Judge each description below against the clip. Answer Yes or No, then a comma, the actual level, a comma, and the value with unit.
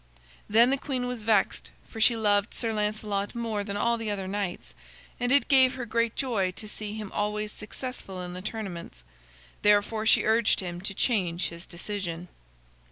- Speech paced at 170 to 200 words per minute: Yes, average, 175 wpm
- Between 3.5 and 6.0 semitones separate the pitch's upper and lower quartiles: No, average, 3.0 semitones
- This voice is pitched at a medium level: No, high, 210 Hz